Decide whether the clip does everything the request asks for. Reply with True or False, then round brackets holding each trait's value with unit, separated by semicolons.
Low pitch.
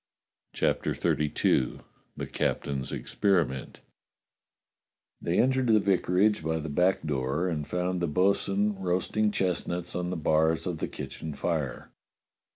True (90 Hz)